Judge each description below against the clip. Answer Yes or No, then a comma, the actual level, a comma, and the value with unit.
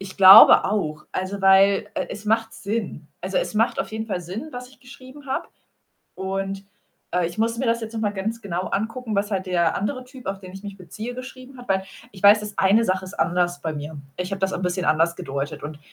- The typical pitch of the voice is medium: No, high, 195 Hz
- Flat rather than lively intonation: No, average, 3.5 semitones